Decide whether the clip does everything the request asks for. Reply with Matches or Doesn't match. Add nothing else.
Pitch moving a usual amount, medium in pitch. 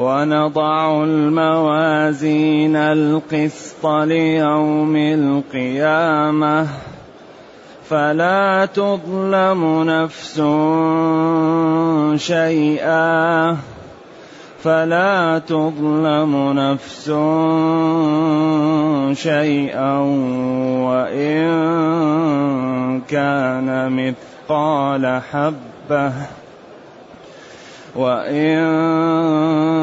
Doesn't match